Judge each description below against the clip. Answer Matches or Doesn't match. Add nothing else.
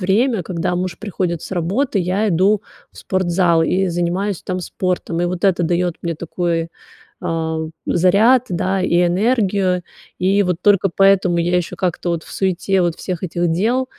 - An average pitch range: Doesn't match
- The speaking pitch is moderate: Matches